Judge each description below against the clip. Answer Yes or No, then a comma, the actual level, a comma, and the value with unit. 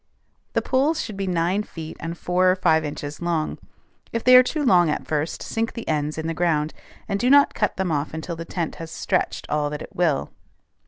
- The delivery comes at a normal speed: No, fast, 220 wpm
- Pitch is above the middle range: No, medium, 170 Hz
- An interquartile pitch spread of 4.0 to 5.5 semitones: Yes, average, 4.5 semitones